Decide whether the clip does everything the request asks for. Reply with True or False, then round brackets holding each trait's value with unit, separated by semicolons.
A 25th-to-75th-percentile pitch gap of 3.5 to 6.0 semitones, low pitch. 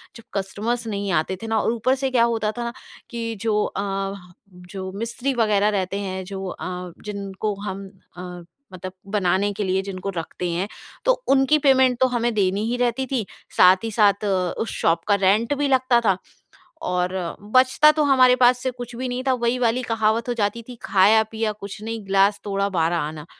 False (3.8 semitones; 210 Hz)